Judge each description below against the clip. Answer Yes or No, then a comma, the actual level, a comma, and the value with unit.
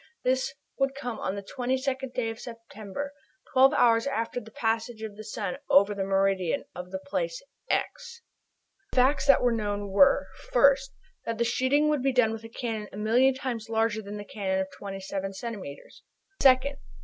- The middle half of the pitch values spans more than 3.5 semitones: Yes, average, 4.4 semitones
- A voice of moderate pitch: No, high, 230 Hz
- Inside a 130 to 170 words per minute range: No, average, 180 wpm